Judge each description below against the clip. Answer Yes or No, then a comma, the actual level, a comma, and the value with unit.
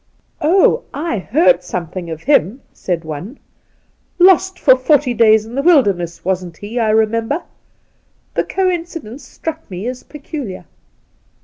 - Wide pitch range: Yes, wide, 8.5 semitones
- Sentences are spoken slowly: No, average, 145 wpm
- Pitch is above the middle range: Yes, high, 240 Hz